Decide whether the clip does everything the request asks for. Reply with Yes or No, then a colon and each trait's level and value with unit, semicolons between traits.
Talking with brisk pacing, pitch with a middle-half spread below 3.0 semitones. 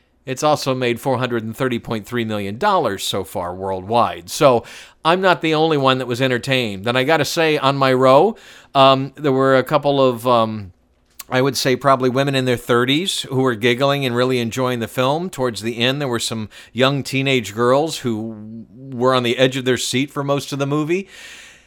No: average, 195 wpm; narrow, 2.5 semitones